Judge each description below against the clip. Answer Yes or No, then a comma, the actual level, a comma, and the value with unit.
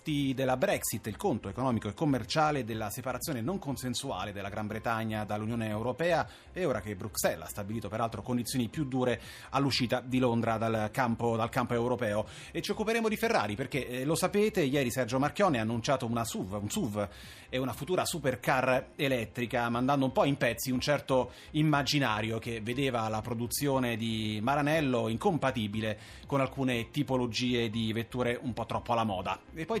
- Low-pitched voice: Yes, low, 125 Hz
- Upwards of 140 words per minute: Yes, fast, 170 wpm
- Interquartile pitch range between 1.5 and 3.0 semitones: No, average, 3.4 semitones